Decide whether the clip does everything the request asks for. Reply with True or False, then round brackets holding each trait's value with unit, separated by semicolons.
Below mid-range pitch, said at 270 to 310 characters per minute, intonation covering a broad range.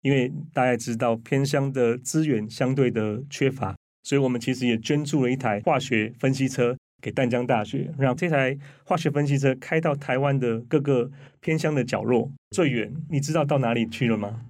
False (130 Hz; 285 characters per minute; 2.8 semitones)